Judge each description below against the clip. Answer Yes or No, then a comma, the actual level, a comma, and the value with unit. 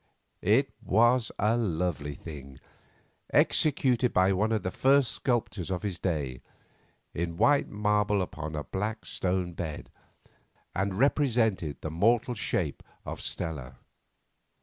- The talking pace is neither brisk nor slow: No, slow, 125 wpm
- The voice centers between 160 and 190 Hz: No, very low, 95 Hz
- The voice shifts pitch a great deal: Yes, wide, 5.9 semitones